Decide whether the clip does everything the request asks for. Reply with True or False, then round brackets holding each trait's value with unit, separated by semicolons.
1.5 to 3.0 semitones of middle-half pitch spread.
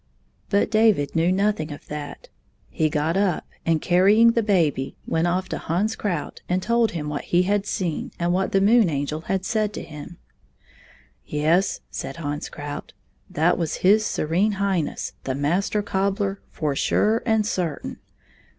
False (4.9 semitones)